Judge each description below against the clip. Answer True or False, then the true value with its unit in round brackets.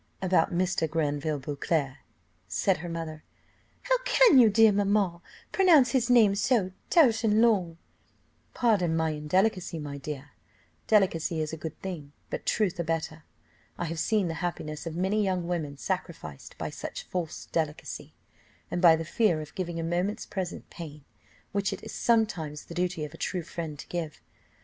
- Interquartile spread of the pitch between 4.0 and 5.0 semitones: True (4.4 semitones)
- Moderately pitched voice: True (175 Hz)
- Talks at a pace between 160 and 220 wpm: True (170 wpm)